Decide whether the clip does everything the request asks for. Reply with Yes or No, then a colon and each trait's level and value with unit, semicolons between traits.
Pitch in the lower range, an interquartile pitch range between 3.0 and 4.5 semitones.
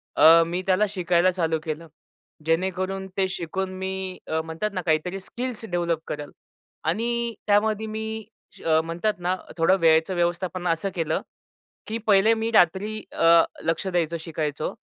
No: medium, 185 Hz; average, 3.5 semitones